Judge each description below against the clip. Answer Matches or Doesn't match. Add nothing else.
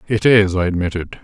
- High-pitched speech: Doesn't match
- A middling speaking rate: Matches